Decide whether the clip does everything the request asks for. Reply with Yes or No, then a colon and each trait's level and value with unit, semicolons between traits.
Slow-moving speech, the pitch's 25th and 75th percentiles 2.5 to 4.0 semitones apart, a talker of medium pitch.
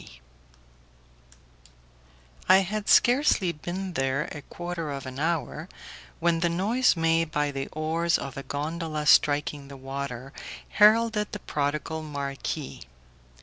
Yes: slow, 120 wpm; average, 3.7 semitones; medium, 160 Hz